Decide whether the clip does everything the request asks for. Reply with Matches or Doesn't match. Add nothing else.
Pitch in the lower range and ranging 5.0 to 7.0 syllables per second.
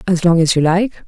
Doesn't match